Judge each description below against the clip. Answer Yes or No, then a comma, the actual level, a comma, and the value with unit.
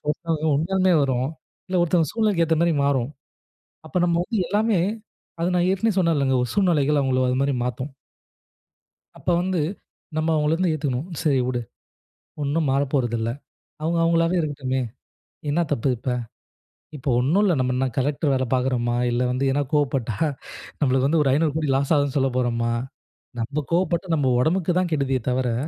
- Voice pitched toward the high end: No, medium, 145 Hz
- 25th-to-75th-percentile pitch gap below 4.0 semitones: No, average, 4.4 semitones